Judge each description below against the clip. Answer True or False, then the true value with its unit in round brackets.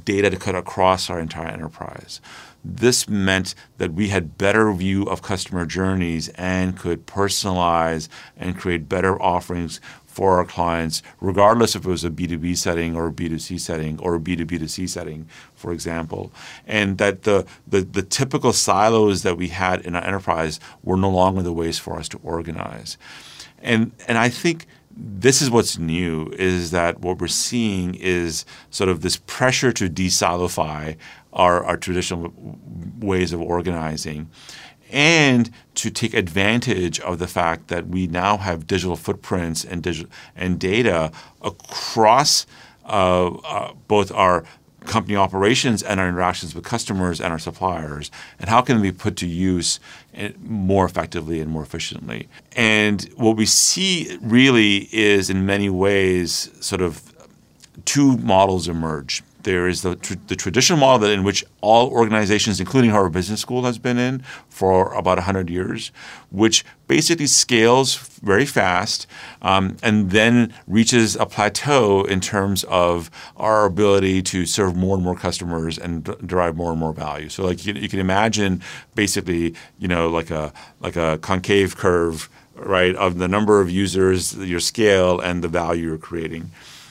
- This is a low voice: True (95 Hz)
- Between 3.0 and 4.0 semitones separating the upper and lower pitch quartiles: True (3.3 semitones)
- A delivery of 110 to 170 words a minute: True (160 wpm)